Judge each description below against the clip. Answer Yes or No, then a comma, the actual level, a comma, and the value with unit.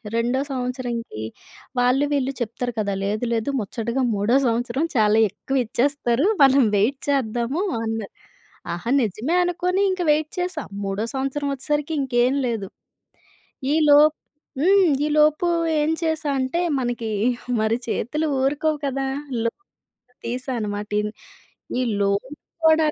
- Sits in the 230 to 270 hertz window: Yes, very high, 255 Hz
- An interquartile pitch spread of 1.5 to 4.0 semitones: No, average, 4.5 semitones